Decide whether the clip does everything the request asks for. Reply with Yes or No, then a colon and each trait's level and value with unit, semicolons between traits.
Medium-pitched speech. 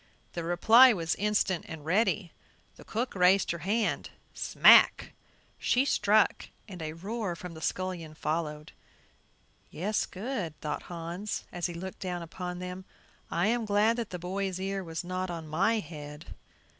Yes: medium, 180 Hz